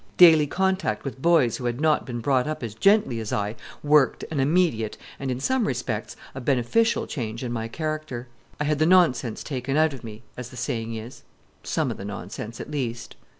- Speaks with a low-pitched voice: Yes, low, 130 Hz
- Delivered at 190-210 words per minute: Yes, average, 200 wpm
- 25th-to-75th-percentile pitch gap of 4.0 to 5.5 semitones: Yes, average, 4.9 semitones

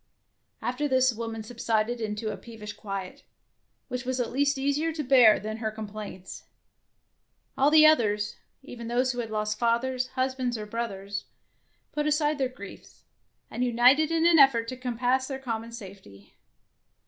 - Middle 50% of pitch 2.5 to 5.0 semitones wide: Yes, average, 3.4 semitones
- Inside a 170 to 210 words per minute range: No, average, 160 wpm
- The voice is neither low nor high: No, high, 240 Hz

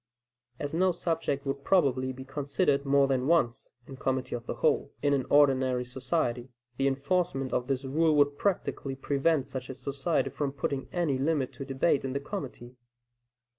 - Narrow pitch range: Yes, narrow, 1.9 semitones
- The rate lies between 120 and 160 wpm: No, average, 170 wpm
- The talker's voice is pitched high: No, low, 135 Hz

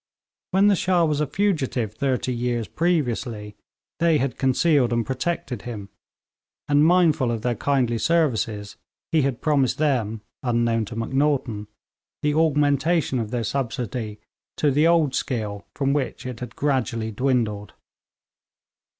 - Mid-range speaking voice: No, low, 130 Hz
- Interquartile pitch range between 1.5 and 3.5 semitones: No, average, 4.6 semitones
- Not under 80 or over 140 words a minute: Yes, slow, 135 wpm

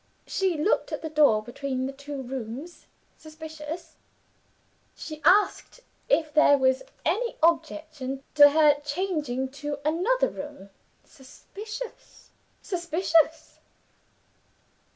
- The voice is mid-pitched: No, very high, 305 Hz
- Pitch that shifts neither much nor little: Yes, average, 3.3 semitones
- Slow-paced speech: Yes, slow, 100 wpm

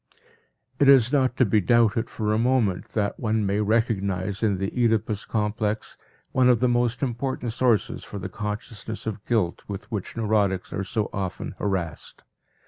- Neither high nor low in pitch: No, low, 110 Hz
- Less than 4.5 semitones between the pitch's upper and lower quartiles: Yes, average, 2.9 semitones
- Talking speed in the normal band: Yes, average, 165 wpm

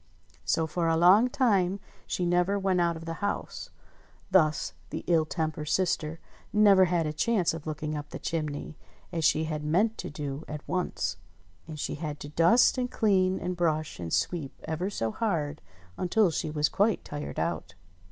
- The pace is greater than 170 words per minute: Yes, average, 180 wpm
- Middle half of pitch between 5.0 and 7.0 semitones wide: No, average, 3.6 semitones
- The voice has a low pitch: No, medium, 165 Hz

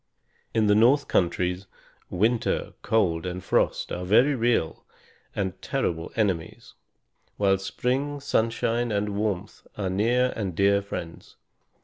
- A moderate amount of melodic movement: Yes, average, 4.2 semitones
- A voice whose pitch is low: Yes, low, 105 Hz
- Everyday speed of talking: No, slow, 120 wpm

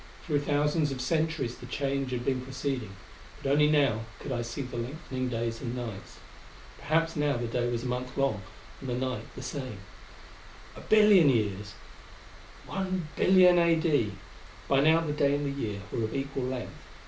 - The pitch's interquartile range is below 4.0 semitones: Yes, average, 3.5 semitones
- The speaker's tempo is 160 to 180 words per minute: Yes, average, 170 wpm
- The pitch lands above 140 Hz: No, low, 135 Hz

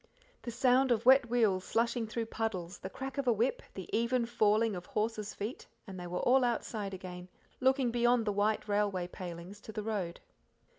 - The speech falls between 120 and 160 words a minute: No, average, 190 wpm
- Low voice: No, high, 220 Hz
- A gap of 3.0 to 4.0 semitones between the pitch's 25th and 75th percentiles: Yes, average, 3.6 semitones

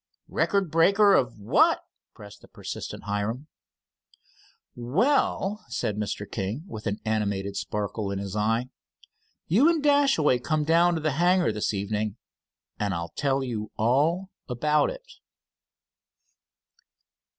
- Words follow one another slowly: Yes, slow, 125 wpm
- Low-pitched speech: Yes, low, 125 Hz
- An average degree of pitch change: No, wide, 8.7 semitones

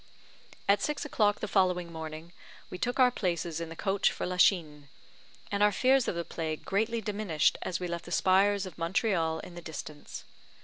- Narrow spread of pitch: No, average, 3.7 semitones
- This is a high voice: No, medium, 180 Hz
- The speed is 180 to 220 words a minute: Yes, average, 185 wpm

